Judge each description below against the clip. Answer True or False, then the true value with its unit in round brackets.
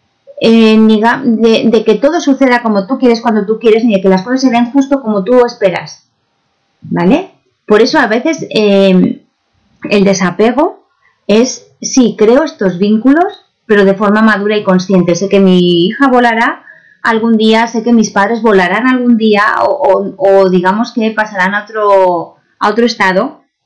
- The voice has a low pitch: False (220 Hz)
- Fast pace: False (175 wpm)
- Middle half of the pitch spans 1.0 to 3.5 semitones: True (3.2 semitones)